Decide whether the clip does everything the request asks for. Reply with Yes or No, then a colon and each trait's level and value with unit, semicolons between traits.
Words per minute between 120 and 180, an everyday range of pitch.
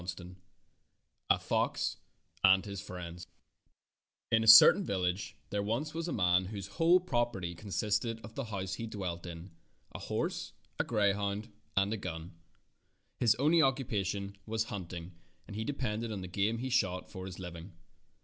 Yes: average, 160 wpm; average, 3.6 semitones